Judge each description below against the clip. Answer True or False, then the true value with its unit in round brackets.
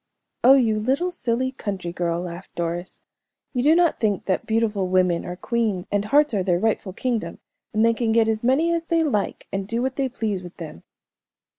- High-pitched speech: True (220 Hz)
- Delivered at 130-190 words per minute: False (200 wpm)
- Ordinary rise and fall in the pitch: False (5.7 semitones)